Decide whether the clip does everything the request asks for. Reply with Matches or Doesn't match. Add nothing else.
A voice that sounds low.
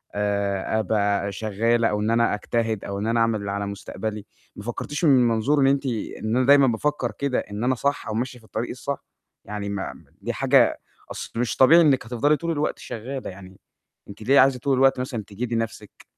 Matches